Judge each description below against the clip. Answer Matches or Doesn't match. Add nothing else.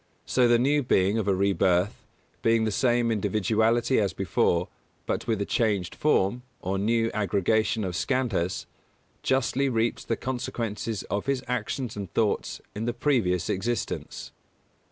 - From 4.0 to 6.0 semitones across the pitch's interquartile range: Doesn't match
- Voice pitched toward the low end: Matches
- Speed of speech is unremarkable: Matches